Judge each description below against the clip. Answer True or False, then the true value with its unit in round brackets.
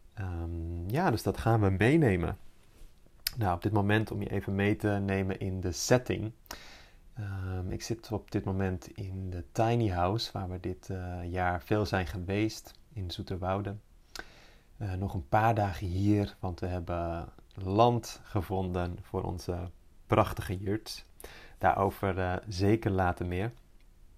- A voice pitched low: True (95 Hz)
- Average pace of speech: True (150 wpm)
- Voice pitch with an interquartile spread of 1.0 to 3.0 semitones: True (2.7 semitones)